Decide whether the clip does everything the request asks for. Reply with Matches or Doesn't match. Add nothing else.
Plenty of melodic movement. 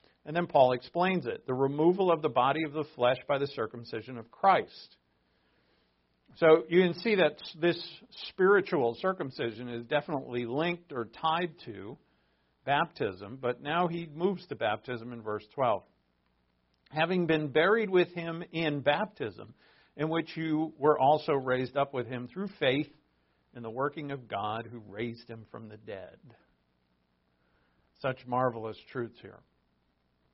Matches